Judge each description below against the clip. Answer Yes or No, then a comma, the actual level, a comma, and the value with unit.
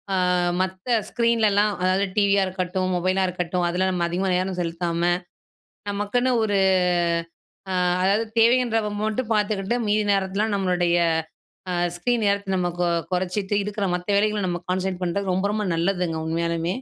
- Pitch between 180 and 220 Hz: Yes, high, 190 Hz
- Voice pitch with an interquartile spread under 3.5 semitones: Yes, average, 2.7 semitones